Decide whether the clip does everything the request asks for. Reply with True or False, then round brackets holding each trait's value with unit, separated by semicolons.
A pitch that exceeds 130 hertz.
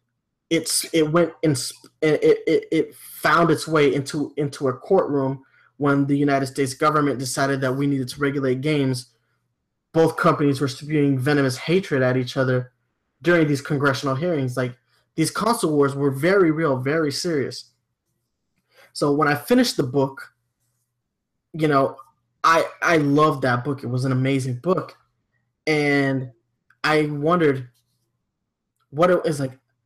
True (140 Hz)